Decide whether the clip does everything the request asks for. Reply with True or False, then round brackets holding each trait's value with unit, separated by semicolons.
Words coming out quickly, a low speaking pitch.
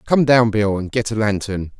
True (235 wpm; 110 Hz)